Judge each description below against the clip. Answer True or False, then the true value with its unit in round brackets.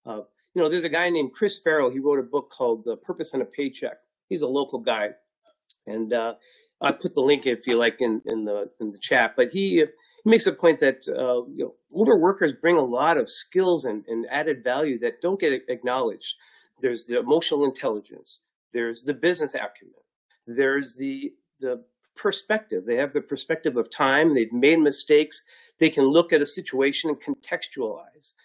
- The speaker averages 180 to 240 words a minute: True (195 wpm)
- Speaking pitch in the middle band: True (150 Hz)